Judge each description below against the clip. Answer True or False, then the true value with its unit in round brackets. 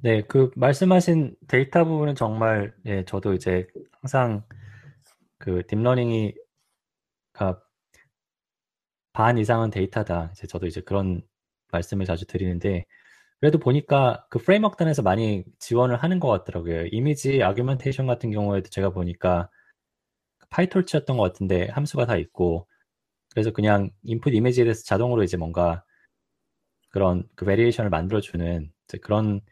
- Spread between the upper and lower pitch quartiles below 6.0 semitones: True (5.3 semitones)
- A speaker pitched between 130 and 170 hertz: False (105 Hz)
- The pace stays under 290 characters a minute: False (315 characters per minute)